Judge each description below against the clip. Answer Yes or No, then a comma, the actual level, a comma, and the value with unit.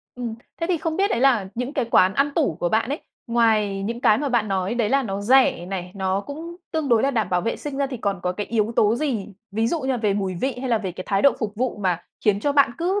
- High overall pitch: Yes, high, 230 Hz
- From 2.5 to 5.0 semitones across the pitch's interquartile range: No, wide, 5.5 semitones